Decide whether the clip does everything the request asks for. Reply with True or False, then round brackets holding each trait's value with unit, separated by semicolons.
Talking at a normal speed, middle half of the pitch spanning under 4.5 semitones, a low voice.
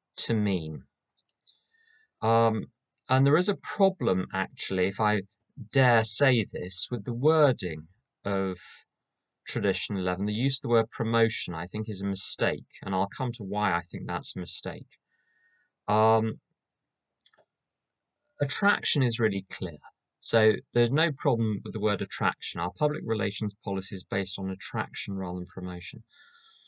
False (145 wpm; 5.2 semitones; 110 Hz)